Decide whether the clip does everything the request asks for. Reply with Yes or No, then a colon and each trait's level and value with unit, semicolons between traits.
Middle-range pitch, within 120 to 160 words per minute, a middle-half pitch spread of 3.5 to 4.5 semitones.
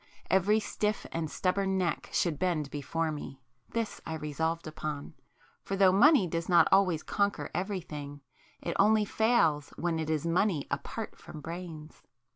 Yes: medium, 170 Hz; average, 145 wpm; average, 4.2 semitones